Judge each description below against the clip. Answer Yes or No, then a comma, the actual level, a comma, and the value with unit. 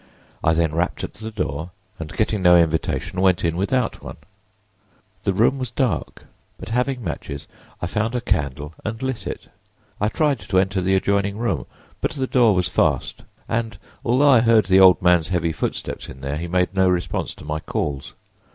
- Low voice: Yes, very low, 95 Hz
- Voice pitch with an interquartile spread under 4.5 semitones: No, average, 5.1 semitones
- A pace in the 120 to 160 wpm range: No, average, 190 wpm